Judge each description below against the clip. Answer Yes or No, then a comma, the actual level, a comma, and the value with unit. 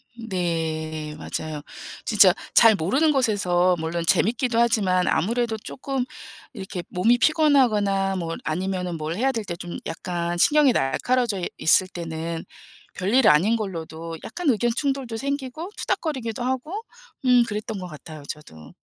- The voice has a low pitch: No, high, 195 Hz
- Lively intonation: Yes, wide, 6.4 semitones